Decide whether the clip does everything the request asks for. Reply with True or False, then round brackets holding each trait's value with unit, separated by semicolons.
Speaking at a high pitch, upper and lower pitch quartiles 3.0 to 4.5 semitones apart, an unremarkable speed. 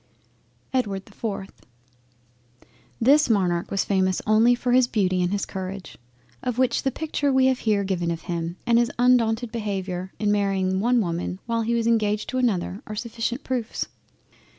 True (215 Hz; 4.2 semitones; 170 wpm)